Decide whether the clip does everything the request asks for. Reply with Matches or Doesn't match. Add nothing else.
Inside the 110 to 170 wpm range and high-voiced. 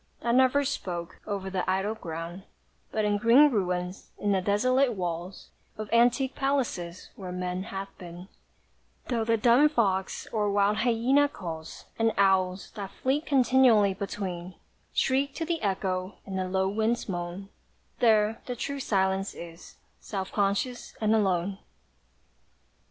Matches